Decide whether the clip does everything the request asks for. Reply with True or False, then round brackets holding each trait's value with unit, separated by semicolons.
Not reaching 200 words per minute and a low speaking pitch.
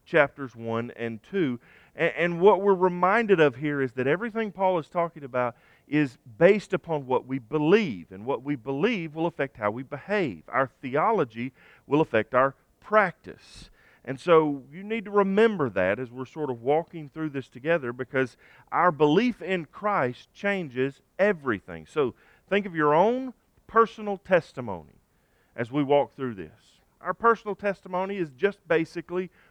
False (160 wpm; 155 Hz)